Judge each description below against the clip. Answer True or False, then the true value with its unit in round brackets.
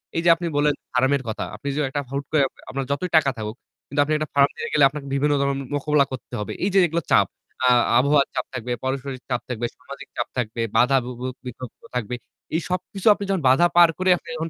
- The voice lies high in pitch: False (140 Hz)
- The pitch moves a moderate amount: True (3.4 semitones)